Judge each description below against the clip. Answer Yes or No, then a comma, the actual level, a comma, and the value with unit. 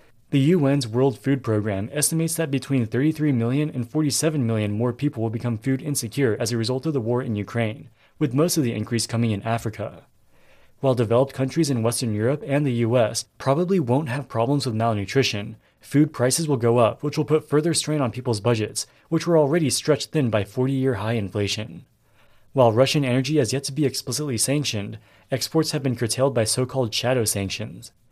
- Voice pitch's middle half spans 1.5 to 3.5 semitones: No, average, 3.9 semitones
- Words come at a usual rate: Yes, average, 195 wpm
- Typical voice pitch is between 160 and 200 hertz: No, low, 130 Hz